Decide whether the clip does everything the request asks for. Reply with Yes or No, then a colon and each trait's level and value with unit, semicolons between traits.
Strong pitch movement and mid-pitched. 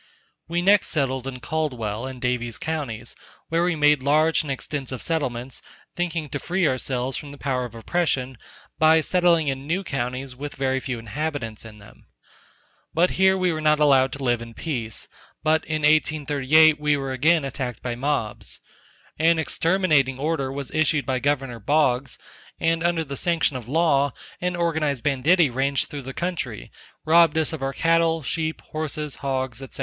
No: average, 3.6 semitones; medium, 145 Hz